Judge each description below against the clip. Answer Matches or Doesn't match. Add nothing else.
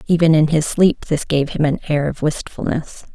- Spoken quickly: Matches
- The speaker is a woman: Matches